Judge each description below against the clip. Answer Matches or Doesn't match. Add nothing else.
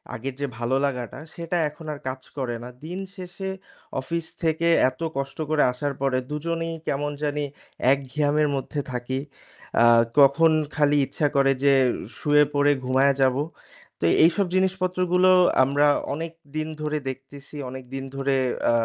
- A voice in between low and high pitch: Matches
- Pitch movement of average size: Matches